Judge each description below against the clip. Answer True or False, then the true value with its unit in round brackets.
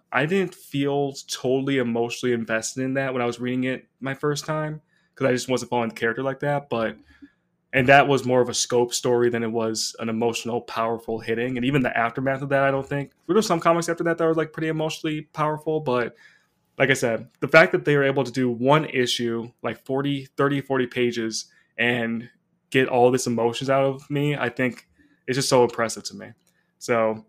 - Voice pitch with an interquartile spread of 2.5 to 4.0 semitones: True (3.2 semitones)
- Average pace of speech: False (215 wpm)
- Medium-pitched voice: False (130 Hz)